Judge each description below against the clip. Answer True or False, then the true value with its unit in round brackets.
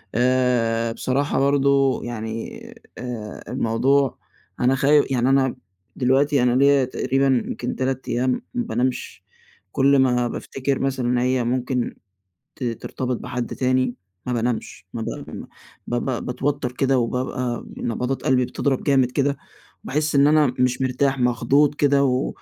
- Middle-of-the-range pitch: False (130 Hz)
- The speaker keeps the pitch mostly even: True (1.9 semitones)